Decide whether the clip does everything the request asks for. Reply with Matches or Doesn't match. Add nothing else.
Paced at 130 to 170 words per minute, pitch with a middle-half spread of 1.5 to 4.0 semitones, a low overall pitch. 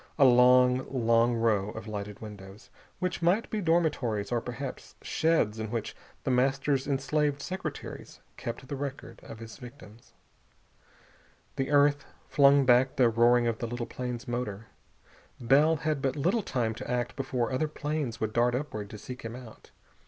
Matches